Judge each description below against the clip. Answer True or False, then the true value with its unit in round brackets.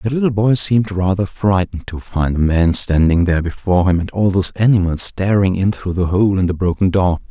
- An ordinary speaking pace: False (220 wpm)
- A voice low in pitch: True (95 Hz)